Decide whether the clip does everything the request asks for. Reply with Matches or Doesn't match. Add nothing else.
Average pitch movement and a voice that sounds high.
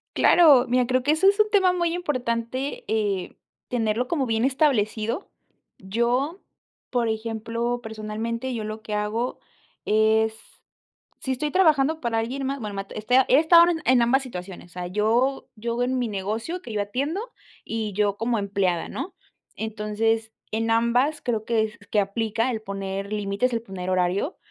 Matches